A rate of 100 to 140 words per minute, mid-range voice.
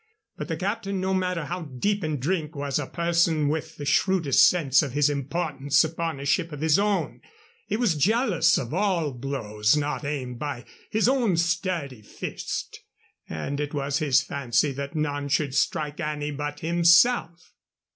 No: average, 165 wpm; medium, 150 Hz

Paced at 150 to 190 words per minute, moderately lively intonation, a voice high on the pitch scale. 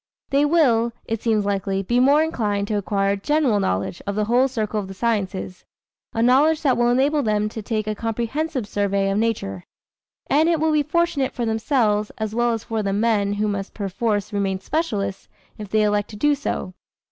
No: average, 200 wpm; average, 4.2 semitones; high, 220 Hz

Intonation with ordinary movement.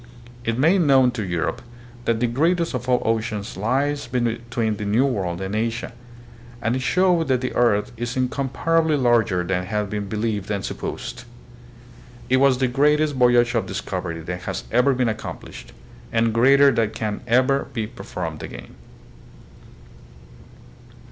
Yes: average, 3.8 semitones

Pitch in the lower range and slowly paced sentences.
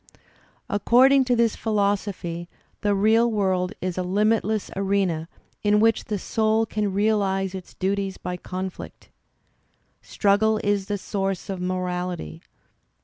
No: high, 200 Hz; slow, 130 wpm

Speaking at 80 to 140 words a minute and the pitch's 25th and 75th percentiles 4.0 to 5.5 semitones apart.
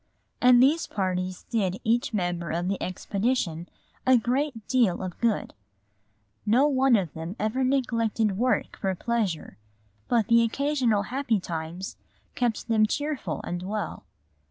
Yes: slow, 135 wpm; average, 5.1 semitones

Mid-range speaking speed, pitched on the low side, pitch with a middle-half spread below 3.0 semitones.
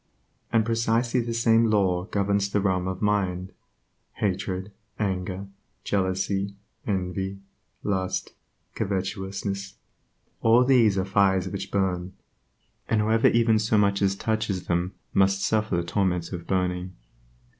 No: slow, 125 wpm; low, 100 Hz; narrow, 2.4 semitones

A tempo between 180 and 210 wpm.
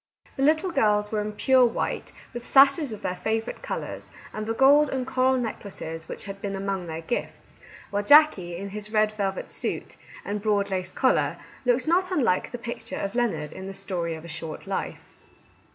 Yes: average, 195 wpm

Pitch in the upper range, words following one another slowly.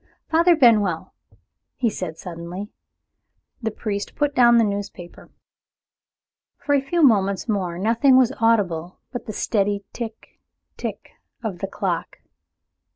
Yes: high, 215 Hz; slow, 125 wpm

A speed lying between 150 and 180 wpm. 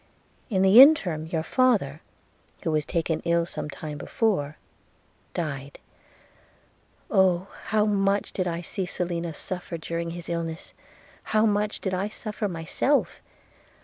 No: average, 140 wpm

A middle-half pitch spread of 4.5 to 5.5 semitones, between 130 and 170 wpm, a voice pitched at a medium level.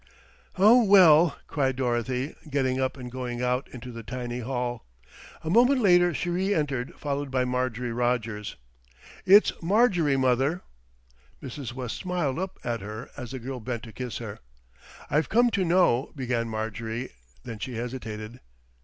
No: average, 4.8 semitones; average, 155 wpm; low, 130 Hz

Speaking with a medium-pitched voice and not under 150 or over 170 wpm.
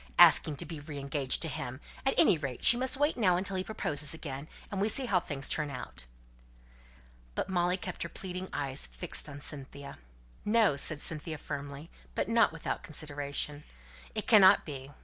No: medium, 155 Hz; average, 180 wpm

